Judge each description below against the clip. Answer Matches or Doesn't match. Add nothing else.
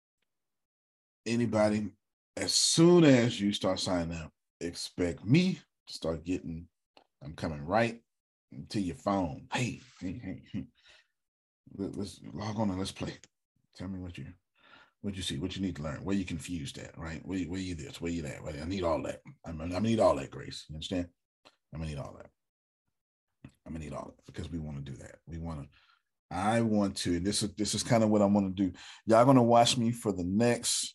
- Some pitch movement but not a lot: Matches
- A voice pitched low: Matches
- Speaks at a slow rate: Doesn't match